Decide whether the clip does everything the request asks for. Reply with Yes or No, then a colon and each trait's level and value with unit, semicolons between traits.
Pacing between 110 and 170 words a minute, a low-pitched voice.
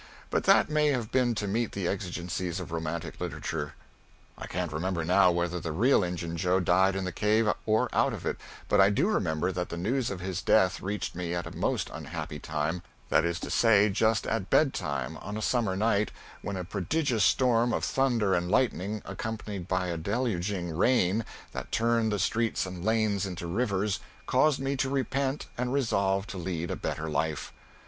No: average, 190 wpm; very low, 95 Hz